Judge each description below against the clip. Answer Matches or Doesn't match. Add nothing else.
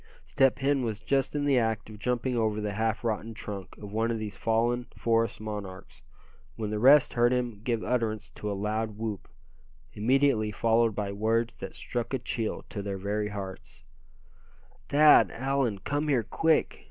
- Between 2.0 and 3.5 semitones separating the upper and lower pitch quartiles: Matches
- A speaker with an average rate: Matches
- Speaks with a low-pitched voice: Matches